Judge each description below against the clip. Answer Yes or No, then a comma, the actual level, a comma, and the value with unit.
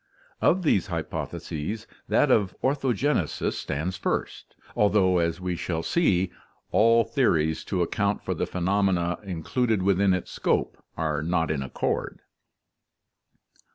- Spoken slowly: Yes, slow, 120 wpm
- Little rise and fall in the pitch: No, average, 4.4 semitones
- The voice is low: Yes, very low, 95 Hz